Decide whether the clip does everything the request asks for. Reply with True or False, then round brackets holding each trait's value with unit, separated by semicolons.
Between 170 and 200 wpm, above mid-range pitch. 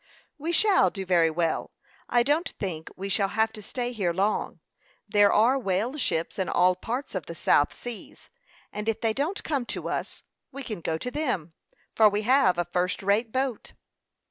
True (190 wpm; 210 Hz)